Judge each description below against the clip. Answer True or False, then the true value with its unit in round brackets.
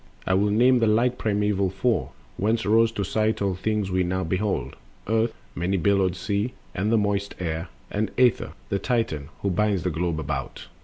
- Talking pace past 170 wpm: True (185 wpm)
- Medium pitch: False (100 Hz)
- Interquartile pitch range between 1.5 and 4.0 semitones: True (2.9 semitones)